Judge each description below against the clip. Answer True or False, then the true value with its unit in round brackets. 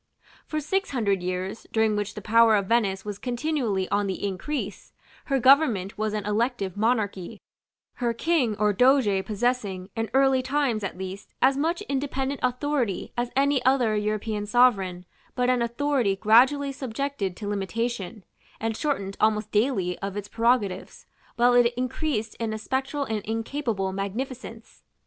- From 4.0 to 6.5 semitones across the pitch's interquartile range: True (4.4 semitones)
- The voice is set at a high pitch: True (225 Hz)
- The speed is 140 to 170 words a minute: True (150 wpm)